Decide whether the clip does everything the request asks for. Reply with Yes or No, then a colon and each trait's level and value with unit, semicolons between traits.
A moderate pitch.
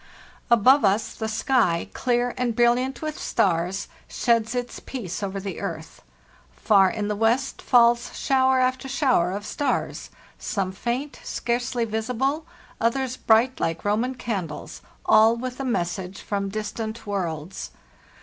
No: high, 230 Hz